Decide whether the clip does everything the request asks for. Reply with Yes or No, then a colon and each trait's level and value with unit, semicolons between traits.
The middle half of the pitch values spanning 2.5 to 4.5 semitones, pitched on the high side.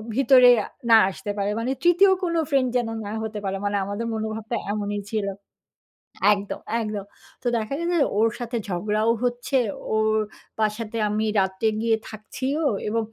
Yes: average, 2.8 semitones; high, 220 Hz